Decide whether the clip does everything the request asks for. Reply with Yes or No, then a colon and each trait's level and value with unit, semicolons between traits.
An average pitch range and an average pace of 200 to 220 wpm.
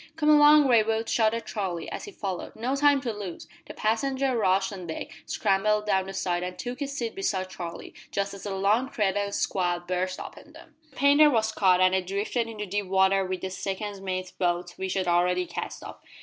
Yes: average, 3.7 semitones; fast, 205 wpm